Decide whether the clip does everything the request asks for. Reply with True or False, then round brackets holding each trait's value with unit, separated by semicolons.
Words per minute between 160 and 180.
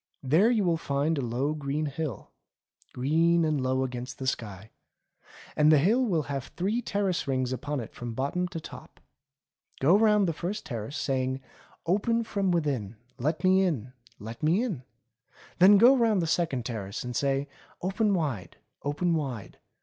True (170 wpm)